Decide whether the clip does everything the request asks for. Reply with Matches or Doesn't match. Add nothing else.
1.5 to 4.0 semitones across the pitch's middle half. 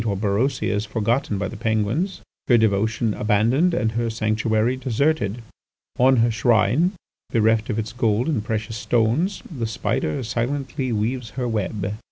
Matches